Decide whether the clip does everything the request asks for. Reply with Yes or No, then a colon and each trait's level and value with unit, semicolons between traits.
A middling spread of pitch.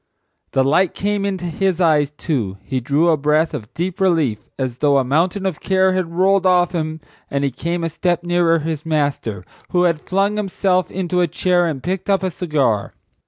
Yes: average, 4.0 semitones